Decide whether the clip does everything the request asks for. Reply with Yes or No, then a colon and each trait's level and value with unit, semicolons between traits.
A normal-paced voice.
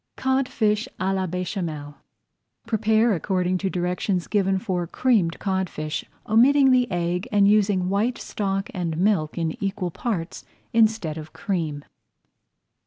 No: slow, 125 wpm